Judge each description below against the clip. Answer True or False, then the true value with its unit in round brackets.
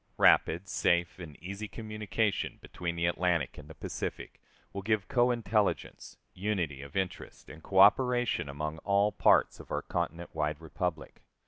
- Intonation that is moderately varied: True (4.6 semitones)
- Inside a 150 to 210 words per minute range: False (140 wpm)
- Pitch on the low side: True (90 Hz)